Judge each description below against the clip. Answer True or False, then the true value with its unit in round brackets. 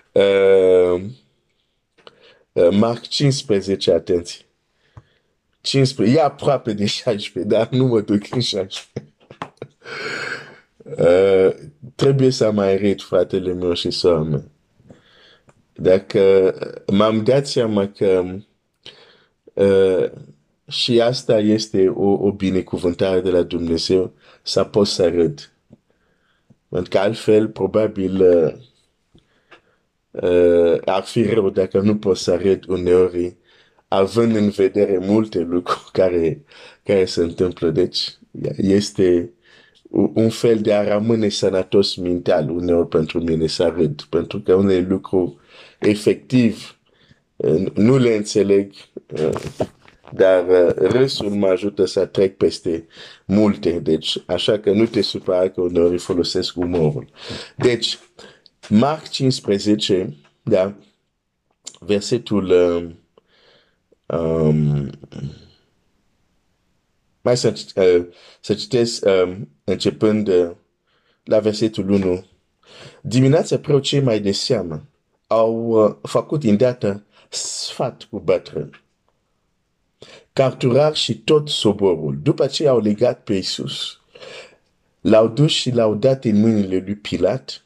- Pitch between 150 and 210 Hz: False (100 Hz)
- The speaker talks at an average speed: False (105 wpm)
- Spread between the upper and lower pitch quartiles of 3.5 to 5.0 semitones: True (4.3 semitones)